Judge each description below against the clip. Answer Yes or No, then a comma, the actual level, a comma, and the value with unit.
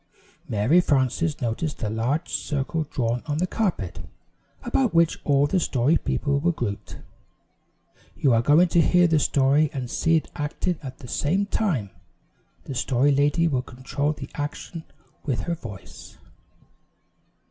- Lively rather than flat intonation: No, average, 4.3 semitones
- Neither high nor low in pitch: Yes, medium, 145 Hz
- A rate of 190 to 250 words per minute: No, average, 145 wpm